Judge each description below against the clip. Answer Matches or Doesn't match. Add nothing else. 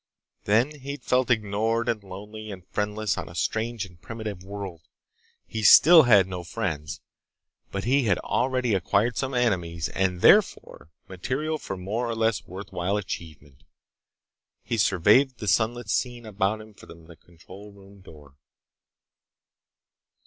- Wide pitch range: Doesn't match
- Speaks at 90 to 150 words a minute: Matches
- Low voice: Matches